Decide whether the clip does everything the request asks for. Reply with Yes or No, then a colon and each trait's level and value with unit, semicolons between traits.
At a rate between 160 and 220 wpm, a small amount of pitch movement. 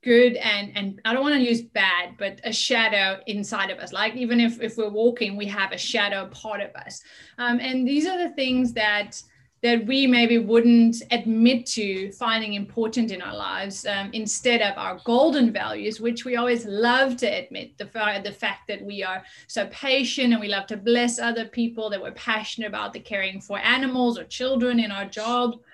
No: average, 200 wpm; average, 3.0 semitones